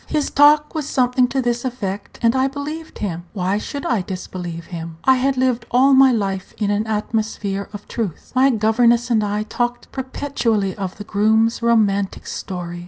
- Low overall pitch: No, high, 225 Hz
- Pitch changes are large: No, average, 4.5 semitones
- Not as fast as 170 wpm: No, average, 175 wpm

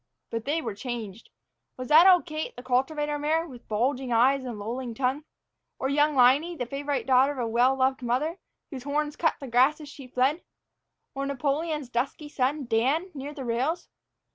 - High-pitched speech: Yes, very high, 270 Hz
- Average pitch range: Yes, average, 3.2 semitones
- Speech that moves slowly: No, average, 185 wpm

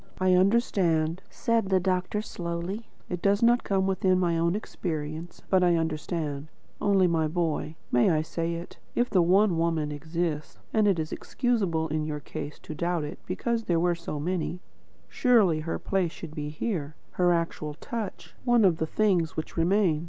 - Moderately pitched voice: Yes, medium, 170 Hz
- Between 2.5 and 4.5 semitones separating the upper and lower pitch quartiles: Yes, average, 3.4 semitones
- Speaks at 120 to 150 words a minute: No, average, 180 wpm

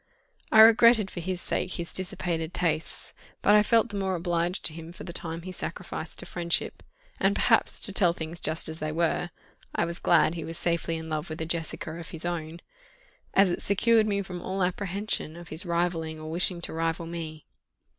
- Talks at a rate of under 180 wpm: No, fast, 205 wpm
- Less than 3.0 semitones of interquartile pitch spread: Yes, narrow, 2.4 semitones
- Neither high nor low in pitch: Yes, medium, 170 Hz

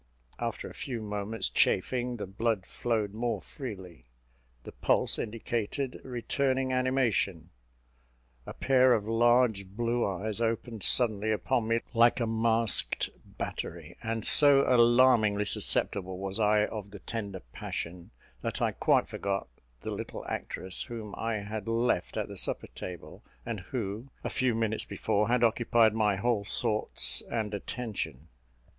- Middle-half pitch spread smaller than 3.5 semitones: Yes, average, 2.8 semitones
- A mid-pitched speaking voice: No, low, 110 Hz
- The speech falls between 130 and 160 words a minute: Yes, average, 140 wpm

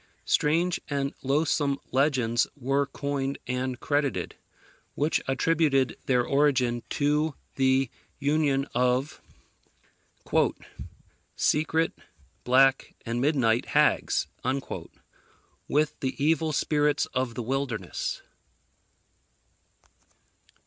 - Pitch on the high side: No, medium, 140 Hz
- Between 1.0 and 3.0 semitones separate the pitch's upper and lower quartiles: Yes, narrow, 2.5 semitones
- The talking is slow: Yes, slow, 80 wpm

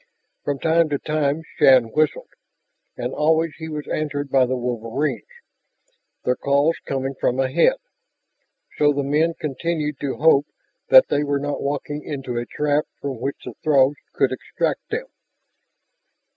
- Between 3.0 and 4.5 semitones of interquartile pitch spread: No, narrow, 2.4 semitones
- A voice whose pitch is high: No, medium, 145 Hz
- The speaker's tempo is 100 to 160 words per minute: Yes, average, 145 wpm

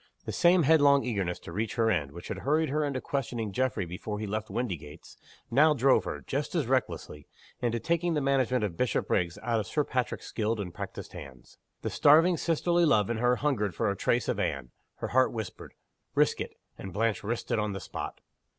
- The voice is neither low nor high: No, low, 120 Hz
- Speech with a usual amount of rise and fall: No, wide, 5.7 semitones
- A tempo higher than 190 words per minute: Yes, fast, 205 wpm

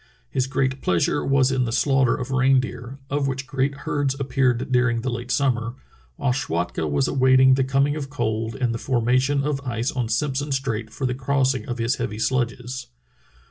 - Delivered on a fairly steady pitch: Yes, narrow, 2.3 semitones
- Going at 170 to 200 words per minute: Yes, average, 180 wpm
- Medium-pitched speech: No, low, 130 Hz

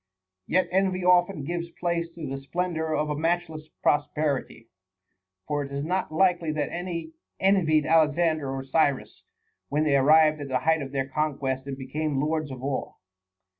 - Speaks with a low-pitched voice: No, medium, 155 Hz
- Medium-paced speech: Yes, average, 165 wpm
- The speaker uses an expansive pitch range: No, average, 3.4 semitones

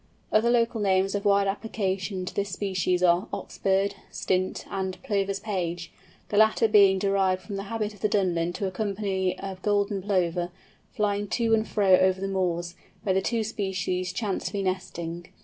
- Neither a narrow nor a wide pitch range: No, narrow, 1.8 semitones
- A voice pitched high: Yes, high, 195 Hz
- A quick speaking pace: No, average, 180 wpm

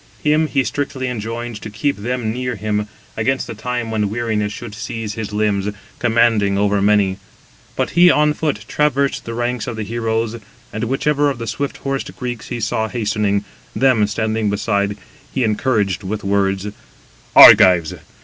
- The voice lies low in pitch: Yes, low, 110 Hz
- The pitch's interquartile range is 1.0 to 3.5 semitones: Yes, average, 3.2 semitones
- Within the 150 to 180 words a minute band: Yes, average, 160 wpm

